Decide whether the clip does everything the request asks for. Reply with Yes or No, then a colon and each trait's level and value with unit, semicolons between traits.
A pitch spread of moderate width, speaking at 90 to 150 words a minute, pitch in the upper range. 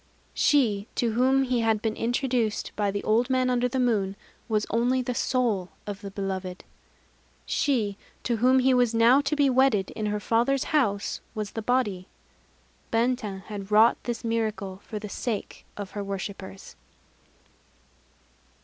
No: average, 3.7 semitones; average, 160 wpm; high, 225 Hz